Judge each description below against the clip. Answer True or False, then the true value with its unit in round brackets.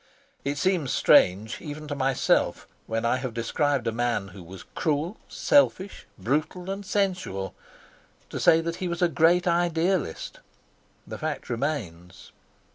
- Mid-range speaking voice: True (145 Hz)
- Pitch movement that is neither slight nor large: False (7.2 semitones)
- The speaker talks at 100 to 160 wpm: True (140 wpm)